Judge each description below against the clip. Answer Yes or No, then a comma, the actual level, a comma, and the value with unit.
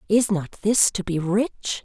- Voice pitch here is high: Yes, high, 200 Hz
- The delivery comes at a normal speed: Yes, average, 195 wpm